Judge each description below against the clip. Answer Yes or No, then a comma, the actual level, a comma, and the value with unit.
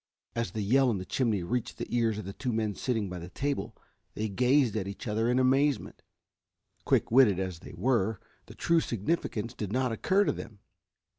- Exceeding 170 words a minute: Yes, average, 200 wpm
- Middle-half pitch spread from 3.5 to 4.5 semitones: Yes, average, 4.2 semitones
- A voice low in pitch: Yes, low, 115 Hz